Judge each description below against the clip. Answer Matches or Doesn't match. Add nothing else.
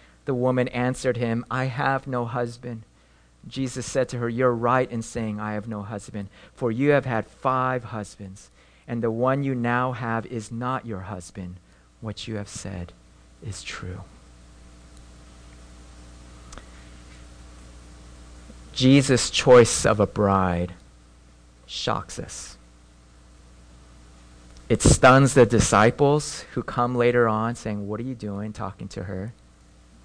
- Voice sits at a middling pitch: Doesn't match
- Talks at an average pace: Doesn't match